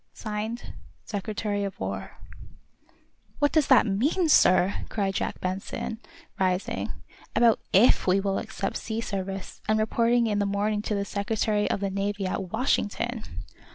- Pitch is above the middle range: Yes, high, 205 Hz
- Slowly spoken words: No, average, 145 wpm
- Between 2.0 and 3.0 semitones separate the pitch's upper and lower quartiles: Yes, narrow, 2.4 semitones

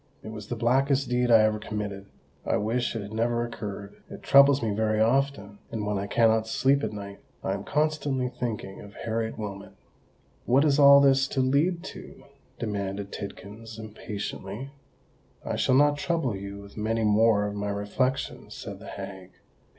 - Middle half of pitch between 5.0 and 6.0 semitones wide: No, average, 4.3 semitones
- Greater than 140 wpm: Yes, average, 170 wpm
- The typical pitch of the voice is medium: No, low, 110 Hz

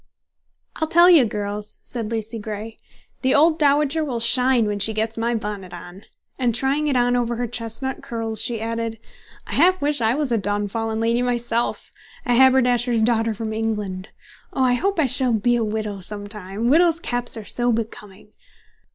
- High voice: Yes, high, 230 Hz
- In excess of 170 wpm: Yes, average, 180 wpm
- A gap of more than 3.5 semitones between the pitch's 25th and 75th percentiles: No, average, 3.0 semitones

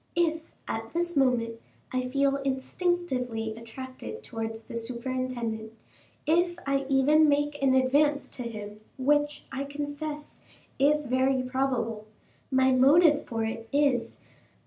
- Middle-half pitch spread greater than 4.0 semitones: No, average, 3.7 semitones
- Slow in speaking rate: Yes, slow, 130 wpm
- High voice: Yes, very high, 265 Hz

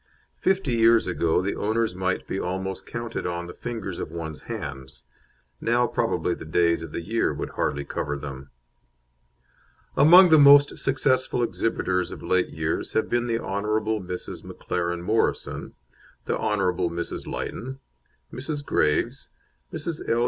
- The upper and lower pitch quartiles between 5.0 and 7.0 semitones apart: Yes, wide, 5.6 semitones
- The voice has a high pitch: No, low, 100 Hz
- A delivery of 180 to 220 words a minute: No, average, 145 wpm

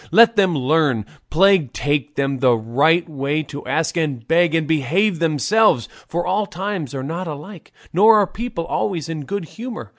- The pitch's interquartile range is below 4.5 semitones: No, average, 5.1 semitones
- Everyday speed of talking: Yes, average, 175 wpm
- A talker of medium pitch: Yes, medium, 165 Hz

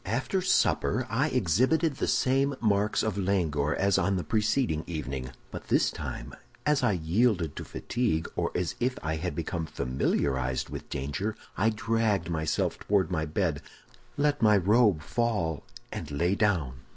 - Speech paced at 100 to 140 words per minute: No, average, 155 wpm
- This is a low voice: Yes, very low, 95 Hz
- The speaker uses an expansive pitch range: Yes, wide, 6.6 semitones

